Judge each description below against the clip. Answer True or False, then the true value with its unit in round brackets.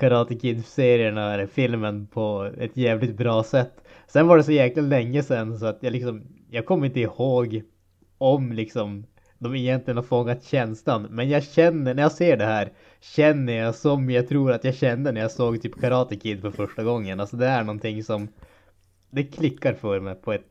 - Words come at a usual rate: False (200 wpm)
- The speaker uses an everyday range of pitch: True (3.5 semitones)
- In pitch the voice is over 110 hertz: True (120 Hz)